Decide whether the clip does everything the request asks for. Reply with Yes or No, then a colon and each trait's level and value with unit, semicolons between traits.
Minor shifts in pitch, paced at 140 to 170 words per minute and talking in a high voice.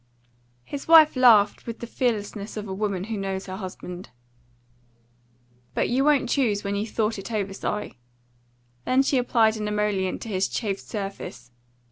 No: average, 3.2 semitones; average, 160 wpm; high, 210 Hz